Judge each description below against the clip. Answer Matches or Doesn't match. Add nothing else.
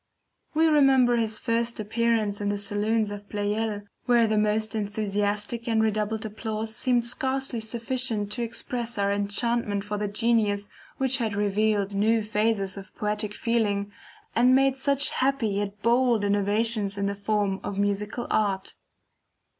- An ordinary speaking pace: Matches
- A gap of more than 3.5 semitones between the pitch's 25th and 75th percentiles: Doesn't match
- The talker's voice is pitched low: Doesn't match